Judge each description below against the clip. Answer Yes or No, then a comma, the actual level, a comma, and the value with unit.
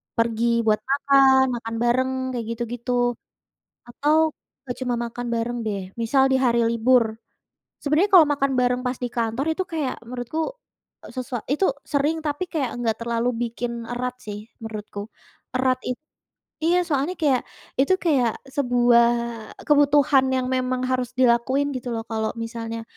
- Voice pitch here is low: No, very high, 250 Hz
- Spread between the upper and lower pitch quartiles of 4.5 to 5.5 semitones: No, average, 2.8 semitones